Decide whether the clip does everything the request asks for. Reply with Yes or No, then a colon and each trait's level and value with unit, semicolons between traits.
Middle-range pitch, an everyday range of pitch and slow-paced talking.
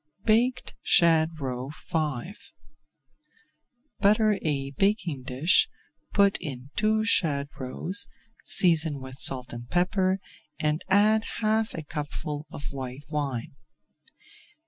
No: medium, 155 Hz; wide, 6.3 semitones; slow, 105 wpm